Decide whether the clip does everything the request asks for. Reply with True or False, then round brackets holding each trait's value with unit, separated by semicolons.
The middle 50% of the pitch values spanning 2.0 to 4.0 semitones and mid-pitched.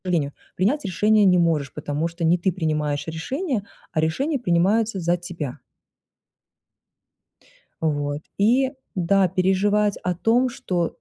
False (4.5 semitones; 180 Hz)